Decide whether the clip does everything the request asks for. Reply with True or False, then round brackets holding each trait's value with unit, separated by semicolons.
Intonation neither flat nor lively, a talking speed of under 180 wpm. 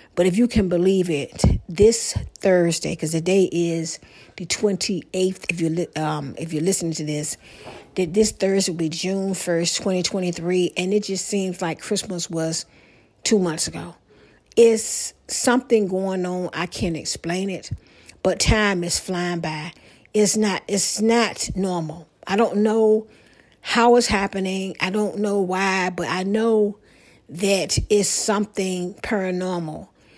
True (3.0 semitones; 150 wpm)